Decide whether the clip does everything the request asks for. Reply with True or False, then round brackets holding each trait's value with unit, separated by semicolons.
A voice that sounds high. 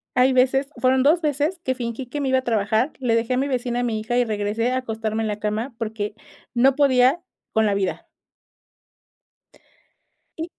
True (245 Hz)